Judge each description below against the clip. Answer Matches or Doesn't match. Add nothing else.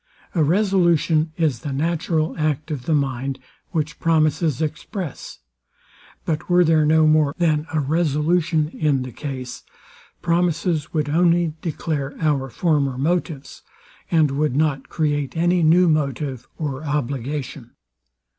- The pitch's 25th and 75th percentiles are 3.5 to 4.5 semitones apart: Doesn't match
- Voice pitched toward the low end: Doesn't match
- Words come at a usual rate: Doesn't match